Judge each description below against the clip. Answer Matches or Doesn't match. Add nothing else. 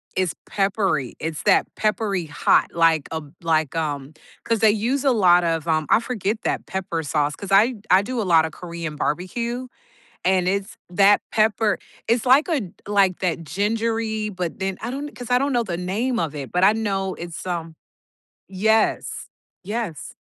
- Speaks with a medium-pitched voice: Doesn't match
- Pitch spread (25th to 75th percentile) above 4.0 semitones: Matches